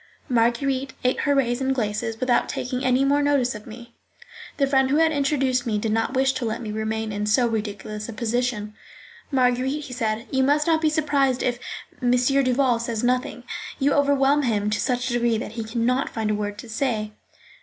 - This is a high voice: Yes, high, 245 Hz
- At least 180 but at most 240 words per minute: Yes, average, 200 wpm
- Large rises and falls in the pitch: No, average, 3.3 semitones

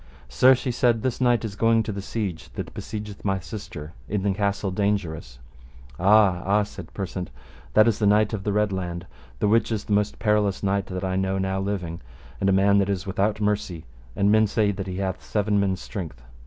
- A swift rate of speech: Yes, fast, 210 wpm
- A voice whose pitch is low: Yes, low, 100 Hz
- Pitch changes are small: Yes, narrow, 1.9 semitones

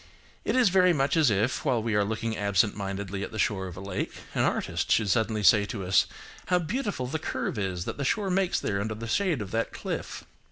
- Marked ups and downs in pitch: Yes, wide, 7.4 semitones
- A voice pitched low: Yes, low, 110 Hz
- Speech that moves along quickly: Yes, fast, 230 wpm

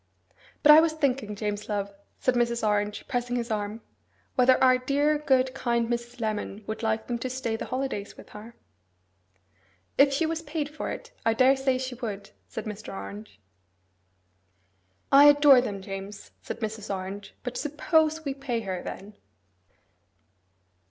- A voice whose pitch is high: Yes, high, 240 Hz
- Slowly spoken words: No, average, 155 wpm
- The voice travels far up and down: No, average, 4.5 semitones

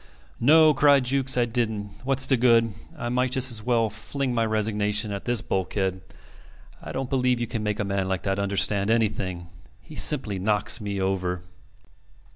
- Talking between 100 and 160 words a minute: No, average, 175 wpm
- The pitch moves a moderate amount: Yes, average, 4.1 semitones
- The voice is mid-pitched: No, low, 110 Hz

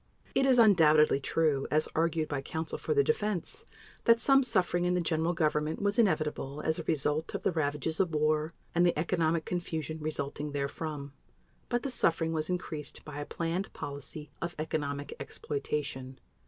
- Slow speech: No, average, 165 wpm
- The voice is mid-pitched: Yes, medium, 160 Hz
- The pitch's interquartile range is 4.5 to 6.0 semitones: No, average, 2.8 semitones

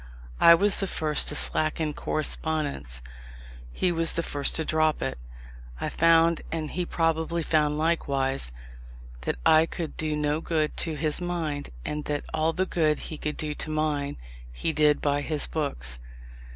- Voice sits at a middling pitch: Yes, medium, 155 Hz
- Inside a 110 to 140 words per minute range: No, average, 165 wpm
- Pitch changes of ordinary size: No, narrow, 1.8 semitones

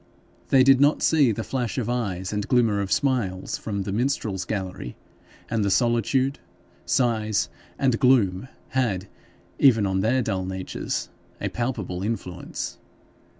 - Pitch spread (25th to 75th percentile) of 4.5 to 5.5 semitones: Yes, average, 4.9 semitones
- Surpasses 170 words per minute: No, average, 140 wpm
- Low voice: Yes, low, 110 Hz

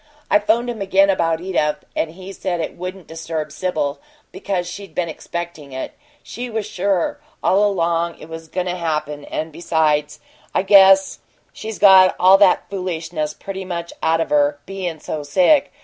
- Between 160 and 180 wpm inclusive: Yes, average, 170 wpm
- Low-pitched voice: No, medium, 175 Hz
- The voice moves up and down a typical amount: Yes, average, 3.2 semitones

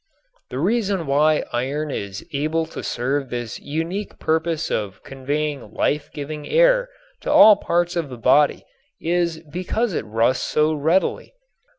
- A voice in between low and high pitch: Yes, medium, 155 Hz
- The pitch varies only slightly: No, average, 4.0 semitones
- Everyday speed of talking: Yes, average, 145 wpm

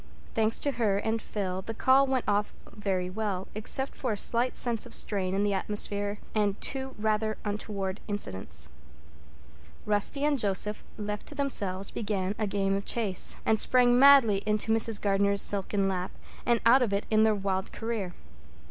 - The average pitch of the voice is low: No, high, 210 Hz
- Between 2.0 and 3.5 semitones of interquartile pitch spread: Yes, narrow, 2.5 semitones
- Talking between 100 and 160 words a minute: No, average, 175 wpm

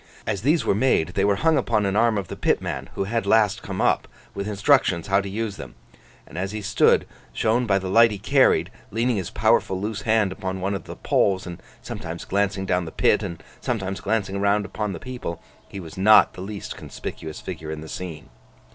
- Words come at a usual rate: No, fast, 215 wpm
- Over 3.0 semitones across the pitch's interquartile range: No, narrow, 2.6 semitones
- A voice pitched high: No, low, 100 Hz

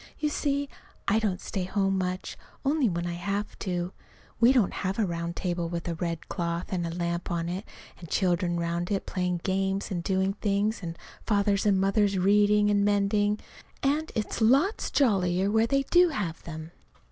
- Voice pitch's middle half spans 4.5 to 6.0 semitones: No, average, 3.1 semitones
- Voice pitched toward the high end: Yes, high, 195 Hz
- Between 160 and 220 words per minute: Yes, average, 185 wpm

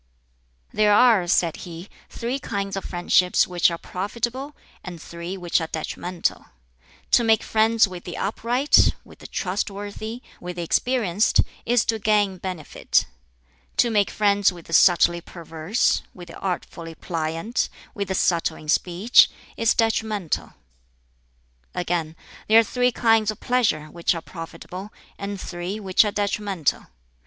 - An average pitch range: Yes, average, 4.1 semitones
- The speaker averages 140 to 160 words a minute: Yes, average, 145 wpm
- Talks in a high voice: Yes, high, 195 Hz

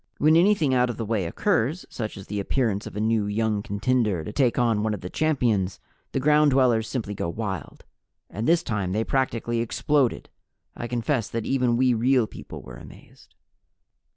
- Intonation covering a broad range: No, average, 3.9 semitones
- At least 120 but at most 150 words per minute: No, average, 185 wpm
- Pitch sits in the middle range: No, low, 115 Hz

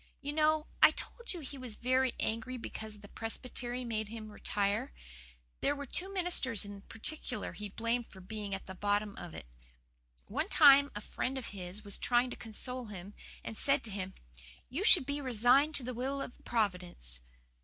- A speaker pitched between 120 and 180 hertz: No, high, 235 Hz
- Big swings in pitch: No, average, 4.8 semitones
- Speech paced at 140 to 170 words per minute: No, average, 185 wpm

